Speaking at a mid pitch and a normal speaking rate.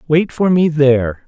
Yes: medium, 145 Hz; average, 190 wpm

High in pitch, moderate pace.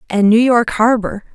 Yes: high, 225 Hz; average, 180 wpm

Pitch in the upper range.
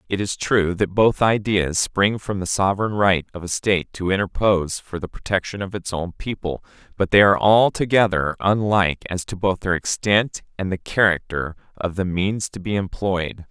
No: very low, 95 Hz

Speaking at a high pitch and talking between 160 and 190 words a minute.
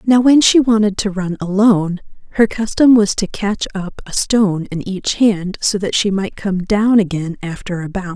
No: high, 200 Hz; fast, 205 wpm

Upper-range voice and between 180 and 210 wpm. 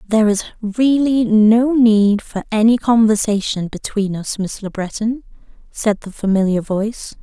No: high, 215 Hz; average, 140 wpm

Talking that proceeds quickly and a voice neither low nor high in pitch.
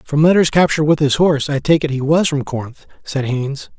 Yes: fast, 240 wpm; medium, 145 Hz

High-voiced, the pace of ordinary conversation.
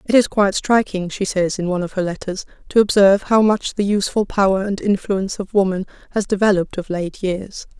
No: high, 195 Hz; fast, 210 wpm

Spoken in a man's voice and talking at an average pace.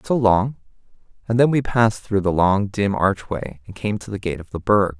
No: male; fast, 230 wpm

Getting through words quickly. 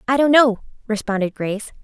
No: average, 165 wpm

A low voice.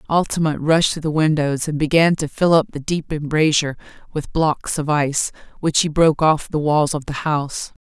No: medium, 155 Hz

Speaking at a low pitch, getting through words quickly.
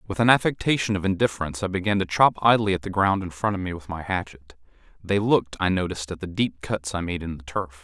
Yes: very low, 95 Hz; fast, 255 wpm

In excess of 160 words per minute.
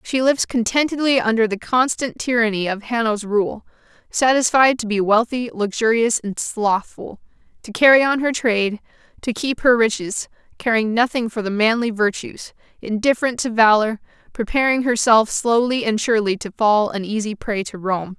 No: average, 155 wpm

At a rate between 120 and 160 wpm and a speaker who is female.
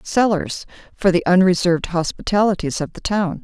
Yes: average, 140 wpm; female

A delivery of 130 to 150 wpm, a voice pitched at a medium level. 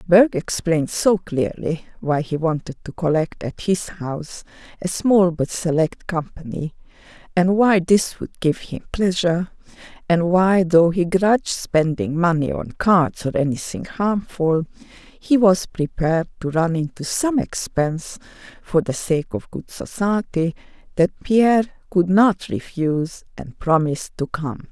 Yes: average, 140 wpm; medium, 175 Hz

